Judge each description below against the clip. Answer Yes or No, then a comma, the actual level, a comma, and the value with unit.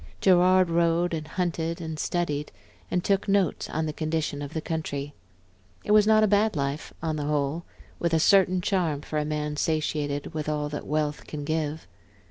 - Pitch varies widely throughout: No, average, 2.9 semitones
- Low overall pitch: No, medium, 160 Hz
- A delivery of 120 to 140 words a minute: No, average, 185 wpm